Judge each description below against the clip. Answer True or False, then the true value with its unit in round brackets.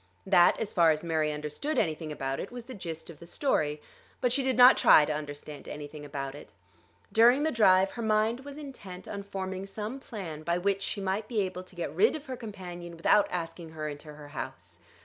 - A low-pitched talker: False (180 Hz)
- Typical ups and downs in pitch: False (6.5 semitones)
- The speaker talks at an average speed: False (215 wpm)